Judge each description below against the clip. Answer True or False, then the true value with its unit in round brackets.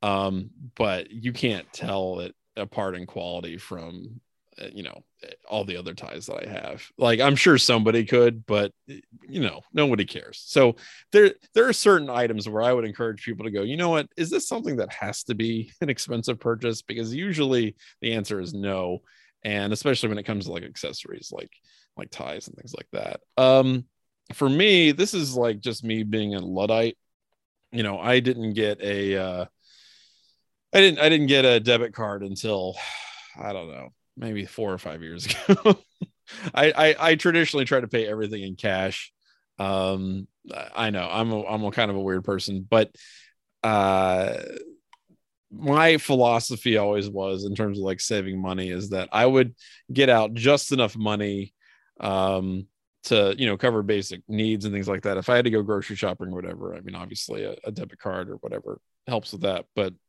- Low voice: True (110 Hz)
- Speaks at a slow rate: False (190 wpm)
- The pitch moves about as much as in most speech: True (4.8 semitones)